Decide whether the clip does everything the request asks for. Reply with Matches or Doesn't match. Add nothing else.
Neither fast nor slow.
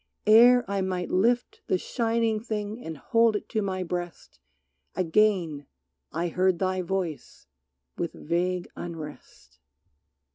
Doesn't match